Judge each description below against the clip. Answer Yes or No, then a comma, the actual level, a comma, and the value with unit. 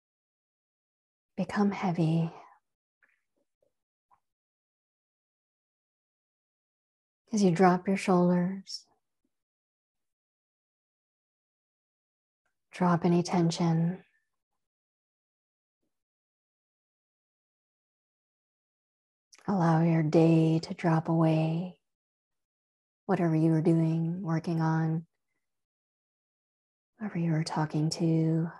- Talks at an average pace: No, slow, 55 wpm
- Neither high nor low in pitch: Yes, medium, 165 Hz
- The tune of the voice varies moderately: No, narrow, 2.1 semitones